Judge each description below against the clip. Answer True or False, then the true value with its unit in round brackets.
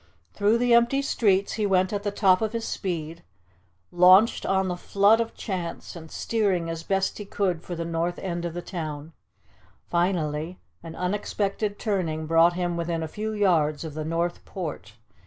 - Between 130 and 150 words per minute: False (175 wpm)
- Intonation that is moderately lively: True (3.5 semitones)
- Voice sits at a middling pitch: True (180 Hz)